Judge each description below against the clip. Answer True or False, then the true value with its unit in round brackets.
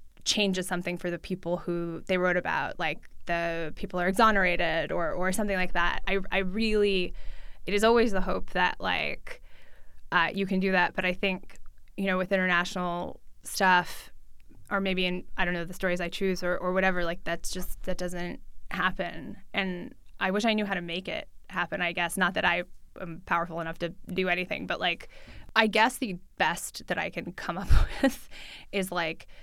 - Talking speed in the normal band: True (195 wpm)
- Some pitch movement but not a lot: False (1.9 semitones)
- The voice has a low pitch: False (185 Hz)